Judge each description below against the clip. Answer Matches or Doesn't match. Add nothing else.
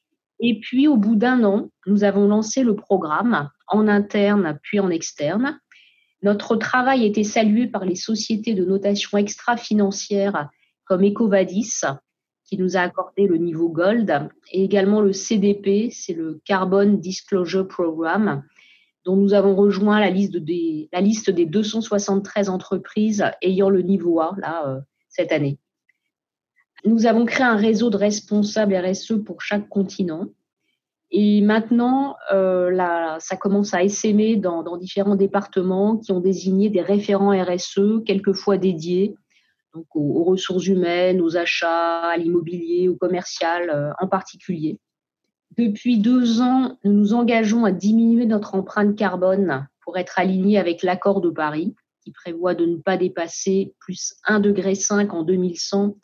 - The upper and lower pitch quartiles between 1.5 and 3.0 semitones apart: Matches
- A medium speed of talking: Doesn't match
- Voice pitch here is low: Doesn't match